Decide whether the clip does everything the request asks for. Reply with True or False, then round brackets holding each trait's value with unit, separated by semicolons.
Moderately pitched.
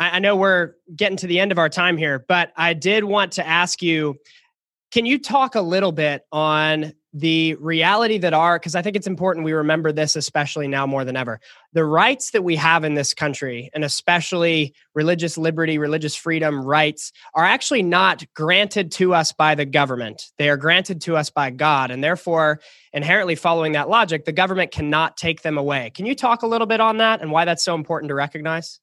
True (165 Hz)